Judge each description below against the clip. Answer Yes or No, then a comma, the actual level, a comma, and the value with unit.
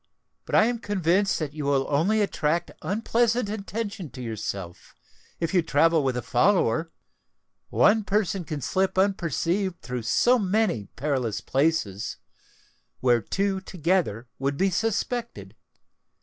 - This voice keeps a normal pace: No, slow, 130 wpm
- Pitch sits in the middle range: Yes, medium, 170 Hz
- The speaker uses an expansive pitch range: Yes, wide, 6.8 semitones